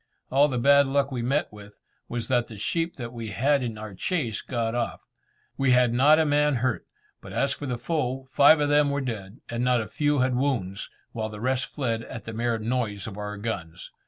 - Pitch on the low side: Yes, low, 125 Hz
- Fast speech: Yes, fast, 215 wpm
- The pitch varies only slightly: No, average, 3.8 semitones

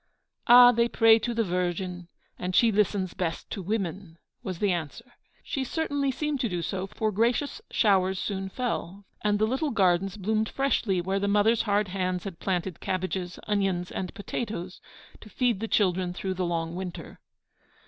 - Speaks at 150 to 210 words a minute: Yes, average, 170 wpm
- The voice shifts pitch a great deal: No, average, 3.6 semitones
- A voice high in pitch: Yes, high, 195 Hz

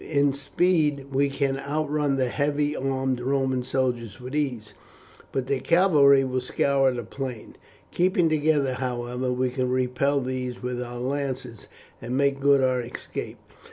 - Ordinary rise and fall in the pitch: No, narrow, 2.0 semitones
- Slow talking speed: No, average, 150 wpm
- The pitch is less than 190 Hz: Yes, low, 135 Hz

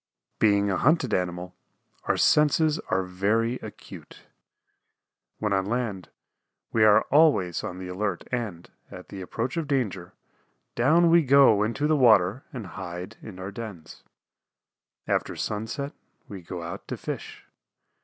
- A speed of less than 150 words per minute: Yes, average, 140 wpm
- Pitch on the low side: Yes, low, 105 Hz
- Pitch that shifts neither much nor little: No, wide, 5.9 semitones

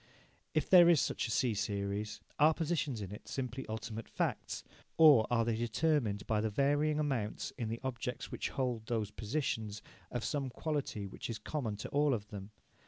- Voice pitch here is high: No, low, 120 Hz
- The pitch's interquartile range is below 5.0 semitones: No, average, 5.3 semitones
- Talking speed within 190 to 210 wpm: No, average, 180 wpm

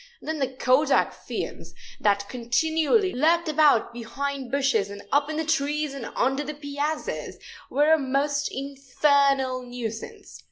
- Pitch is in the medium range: No, very high, 280 Hz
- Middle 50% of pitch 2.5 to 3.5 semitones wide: Yes, average, 2.9 semitones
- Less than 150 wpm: Yes, slow, 135 wpm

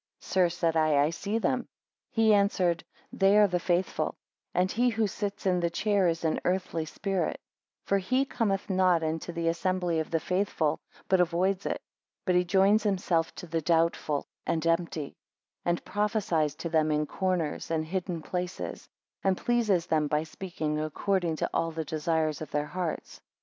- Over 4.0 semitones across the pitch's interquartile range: No, average, 3.2 semitones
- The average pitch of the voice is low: No, medium, 175 Hz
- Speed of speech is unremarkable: Yes, average, 175 wpm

